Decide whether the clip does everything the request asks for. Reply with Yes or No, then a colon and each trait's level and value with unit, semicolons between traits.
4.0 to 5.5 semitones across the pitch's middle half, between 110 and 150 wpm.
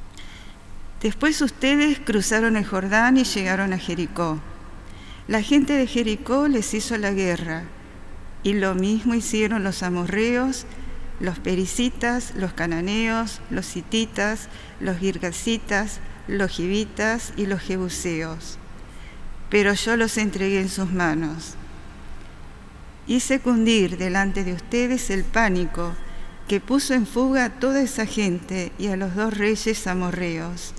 Yes: average, 4.4 semitones; slow, 125 wpm